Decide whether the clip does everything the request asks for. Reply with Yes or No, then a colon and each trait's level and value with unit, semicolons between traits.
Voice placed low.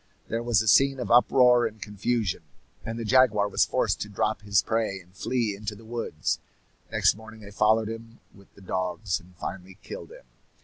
Yes: low, 110 Hz